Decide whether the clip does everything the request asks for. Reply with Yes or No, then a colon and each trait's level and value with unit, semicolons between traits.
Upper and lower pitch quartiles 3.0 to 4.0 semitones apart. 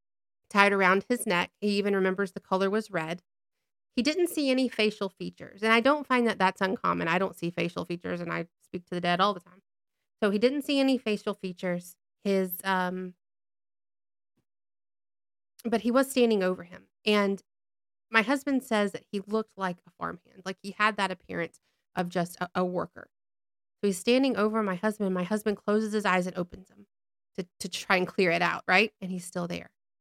Yes: average, 3.3 semitones